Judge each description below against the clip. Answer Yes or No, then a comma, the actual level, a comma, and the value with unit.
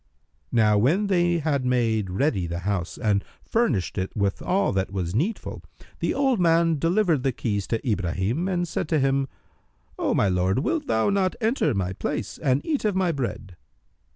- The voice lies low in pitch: Yes, low, 130 Hz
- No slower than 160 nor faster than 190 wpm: Yes, average, 180 wpm